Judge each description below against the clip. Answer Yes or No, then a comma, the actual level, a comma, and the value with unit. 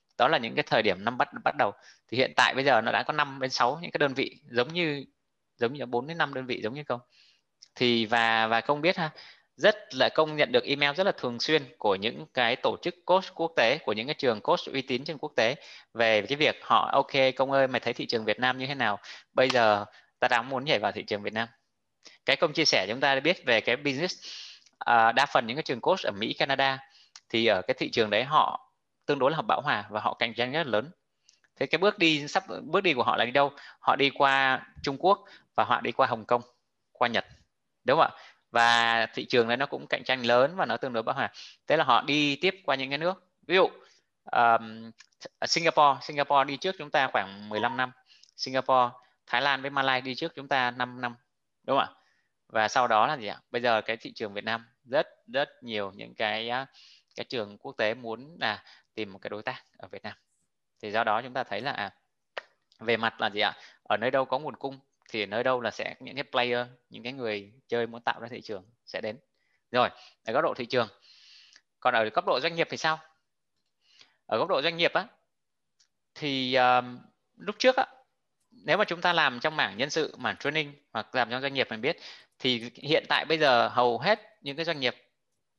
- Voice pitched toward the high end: No, low, 130 Hz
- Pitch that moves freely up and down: No, average, 3.9 semitones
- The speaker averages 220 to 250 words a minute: Yes, average, 240 wpm